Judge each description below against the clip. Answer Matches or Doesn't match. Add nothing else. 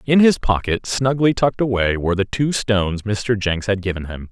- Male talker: Matches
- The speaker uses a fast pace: Matches